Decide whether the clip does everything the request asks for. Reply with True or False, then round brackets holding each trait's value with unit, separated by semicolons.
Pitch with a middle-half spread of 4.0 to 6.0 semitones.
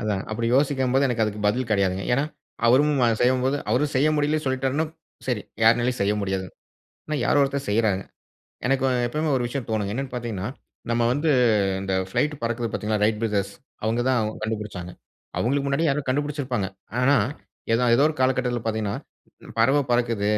True (4.3 semitones)